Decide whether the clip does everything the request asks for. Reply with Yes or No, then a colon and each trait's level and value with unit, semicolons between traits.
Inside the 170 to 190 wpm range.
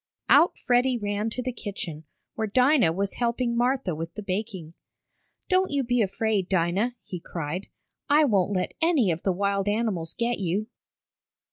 No: average, 160 wpm